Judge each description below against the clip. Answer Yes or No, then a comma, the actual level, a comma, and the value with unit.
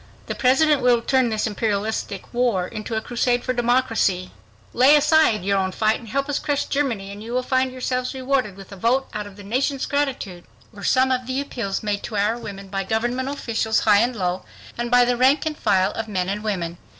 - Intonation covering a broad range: No, average, 4.2 semitones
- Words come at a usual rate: No, fast, 215 wpm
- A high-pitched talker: Yes, high, 235 Hz